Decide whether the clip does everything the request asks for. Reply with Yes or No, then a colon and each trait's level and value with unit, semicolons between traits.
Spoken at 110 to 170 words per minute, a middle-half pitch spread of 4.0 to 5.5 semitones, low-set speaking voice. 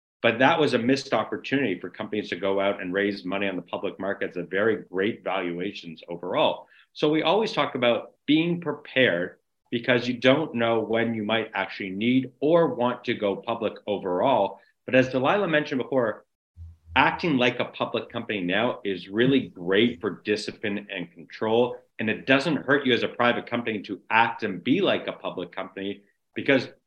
No: average, 180 wpm; average, 4.8 semitones; low, 115 Hz